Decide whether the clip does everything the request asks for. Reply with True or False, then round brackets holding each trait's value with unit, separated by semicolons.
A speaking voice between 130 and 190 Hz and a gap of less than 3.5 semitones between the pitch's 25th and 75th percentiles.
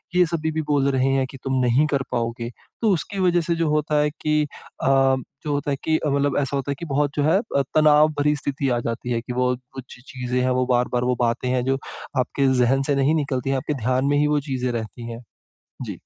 True (135 Hz; 2.9 semitones)